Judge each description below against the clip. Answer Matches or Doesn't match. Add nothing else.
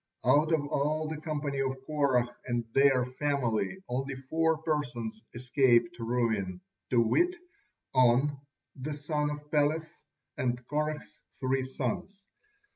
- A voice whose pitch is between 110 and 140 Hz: Matches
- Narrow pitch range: Doesn't match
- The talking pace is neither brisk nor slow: Doesn't match